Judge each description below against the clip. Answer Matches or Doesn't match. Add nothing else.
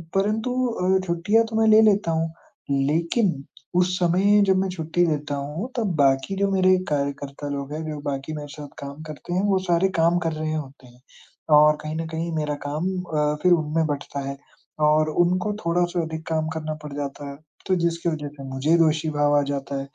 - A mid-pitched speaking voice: Matches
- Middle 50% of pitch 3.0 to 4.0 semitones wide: Matches